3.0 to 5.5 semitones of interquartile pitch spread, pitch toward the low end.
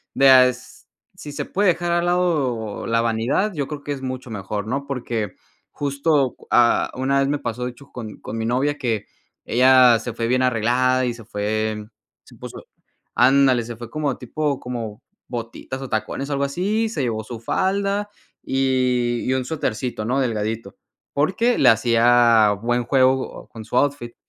Yes: average, 3.4 semitones; low, 125 Hz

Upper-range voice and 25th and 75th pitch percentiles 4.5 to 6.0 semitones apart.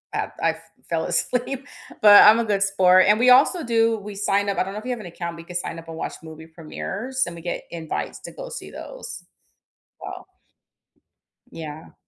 Yes: high, 195 Hz; wide, 5.6 semitones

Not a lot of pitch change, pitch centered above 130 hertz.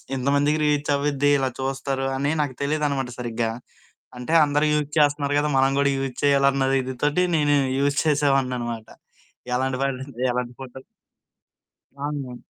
Yes: narrow, 1.9 semitones; medium, 140 Hz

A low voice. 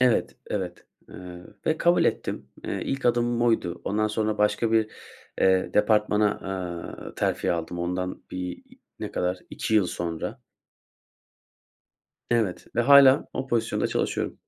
Yes: low, 105 Hz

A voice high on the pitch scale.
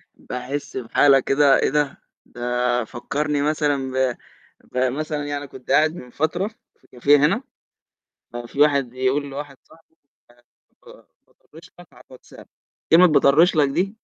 No: medium, 140 Hz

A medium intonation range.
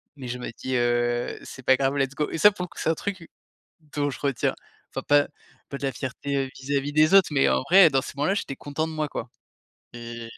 Yes: average, 3.0 semitones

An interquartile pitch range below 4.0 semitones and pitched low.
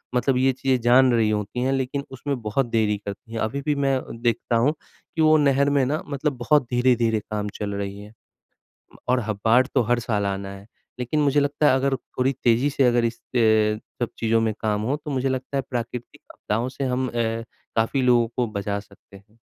Yes: average, 3.5 semitones; low, 120 Hz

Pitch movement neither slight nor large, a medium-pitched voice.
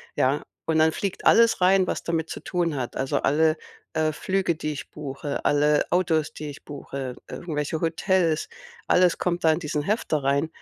Yes: average, 3.0 semitones; medium, 155 Hz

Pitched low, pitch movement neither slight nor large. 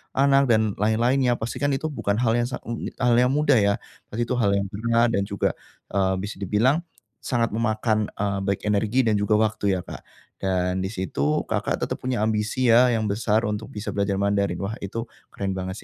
Yes: low, 110 Hz; average, 3.1 semitones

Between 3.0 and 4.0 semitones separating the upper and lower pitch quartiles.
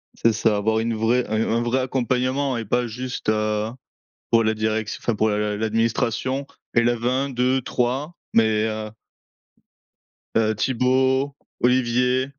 No: narrow, 2.6 semitones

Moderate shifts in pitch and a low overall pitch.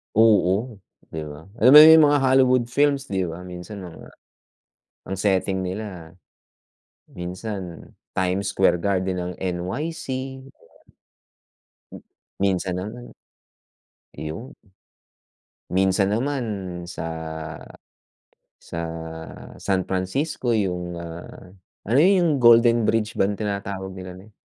Yes: average, 4.4 semitones; very low, 95 Hz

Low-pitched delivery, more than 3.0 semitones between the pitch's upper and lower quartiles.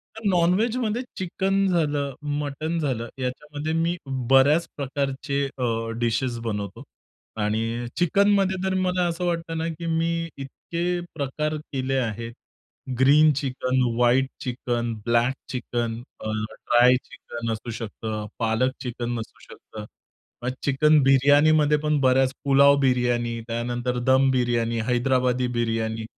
Yes: low, 130 Hz; average, 4.7 semitones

